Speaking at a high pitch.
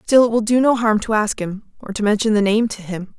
Yes: high, 215 Hz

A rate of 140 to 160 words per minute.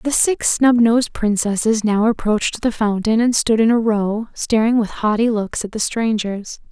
No: average, 180 wpm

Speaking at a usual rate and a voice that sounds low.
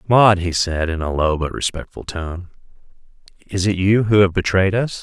Yes: average, 190 wpm; very low, 95 Hz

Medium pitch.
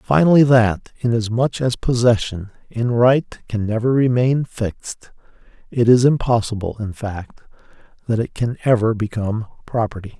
No: low, 115 Hz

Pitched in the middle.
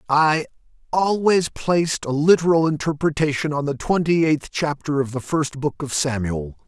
Yes: medium, 150 Hz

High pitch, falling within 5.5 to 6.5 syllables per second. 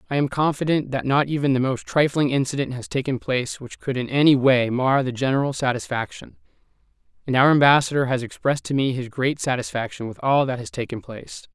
No: low, 130 Hz; 6.0 syllables/s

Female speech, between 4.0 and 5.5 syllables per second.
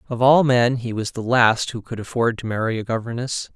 No: male; 5.3 syllables/s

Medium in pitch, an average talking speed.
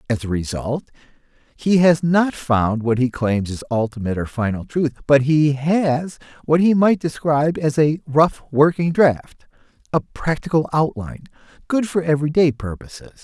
Yes: medium, 145 Hz; average, 155 wpm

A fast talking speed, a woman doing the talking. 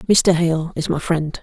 Yes: fast, 210 wpm; female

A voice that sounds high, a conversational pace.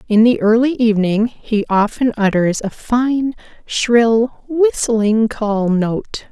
No: high, 225 Hz; slow, 125 wpm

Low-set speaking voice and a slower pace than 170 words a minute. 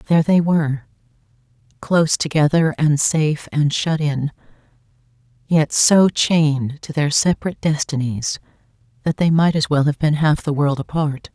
No: medium, 145 Hz; average, 150 wpm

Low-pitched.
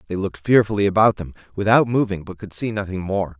Yes: low, 100 Hz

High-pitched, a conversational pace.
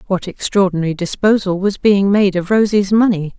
Yes: high, 195 Hz; average, 160 wpm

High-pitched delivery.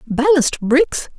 Yes: very high, 285 Hz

